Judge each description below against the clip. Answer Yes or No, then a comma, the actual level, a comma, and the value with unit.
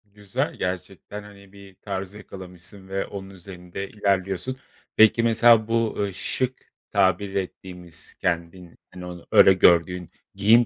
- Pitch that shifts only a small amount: Yes, narrow, 2.2 semitones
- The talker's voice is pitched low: Yes, very low, 95 Hz